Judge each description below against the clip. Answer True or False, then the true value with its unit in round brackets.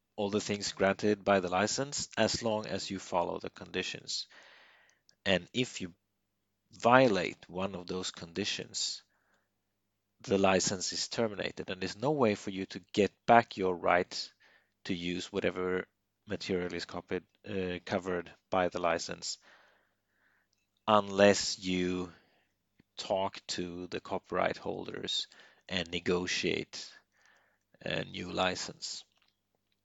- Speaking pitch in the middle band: False (95 Hz)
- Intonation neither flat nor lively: False (2.0 semitones)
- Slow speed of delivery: True (120 wpm)